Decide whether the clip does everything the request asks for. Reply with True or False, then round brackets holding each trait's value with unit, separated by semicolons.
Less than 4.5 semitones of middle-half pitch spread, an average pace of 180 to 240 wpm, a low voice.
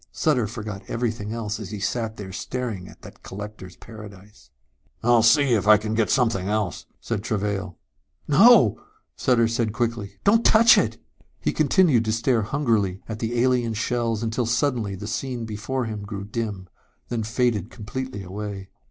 False (2.8 semitones; 160 wpm; 110 Hz)